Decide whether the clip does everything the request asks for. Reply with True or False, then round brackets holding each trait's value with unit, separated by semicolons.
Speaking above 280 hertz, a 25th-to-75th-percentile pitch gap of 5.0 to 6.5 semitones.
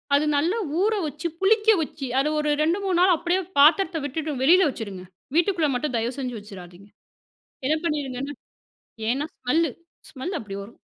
True (300 Hz; 5.3 semitones)